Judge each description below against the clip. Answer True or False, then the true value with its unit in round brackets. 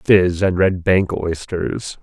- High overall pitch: False (90 Hz)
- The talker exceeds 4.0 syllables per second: False (3.1 syllables/s)